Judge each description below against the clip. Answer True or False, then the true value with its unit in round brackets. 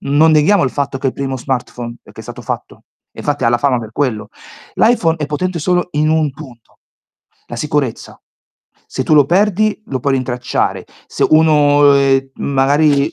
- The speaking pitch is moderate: True (145 Hz)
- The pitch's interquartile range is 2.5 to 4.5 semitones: True (2.8 semitones)